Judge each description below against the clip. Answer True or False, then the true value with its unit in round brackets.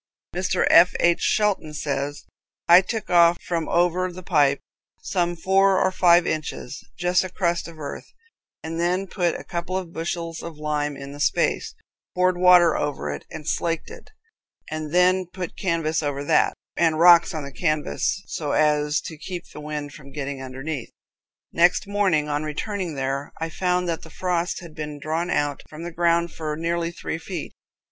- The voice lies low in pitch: False (165 Hz)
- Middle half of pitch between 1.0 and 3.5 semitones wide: True (3.0 semitones)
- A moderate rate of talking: True (175 wpm)